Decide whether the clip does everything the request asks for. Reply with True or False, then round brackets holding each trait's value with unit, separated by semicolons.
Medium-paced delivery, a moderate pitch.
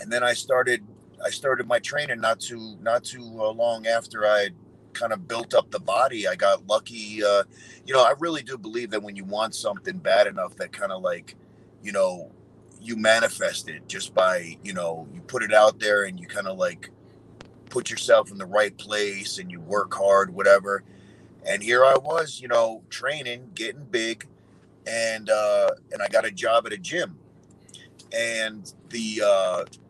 False (190 wpm; 110 Hz)